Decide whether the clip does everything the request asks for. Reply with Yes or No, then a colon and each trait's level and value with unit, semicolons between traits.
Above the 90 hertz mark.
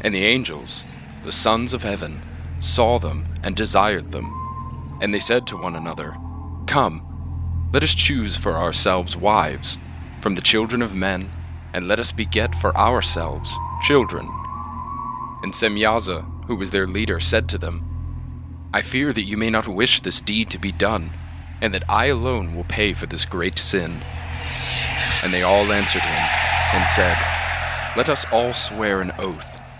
No: very low, 85 Hz